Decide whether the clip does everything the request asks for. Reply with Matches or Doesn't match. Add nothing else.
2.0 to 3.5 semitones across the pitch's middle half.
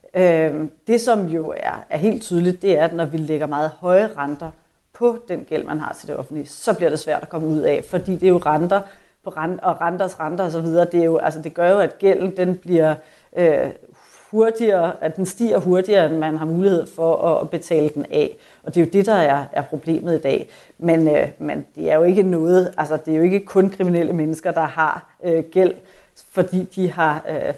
Matches